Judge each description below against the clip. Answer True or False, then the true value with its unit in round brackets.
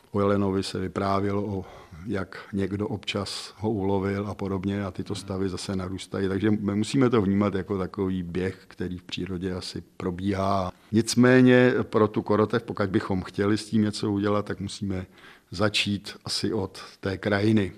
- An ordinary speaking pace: True (160 wpm)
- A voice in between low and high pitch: False (100 Hz)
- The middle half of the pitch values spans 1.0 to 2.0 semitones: True (1.7 semitones)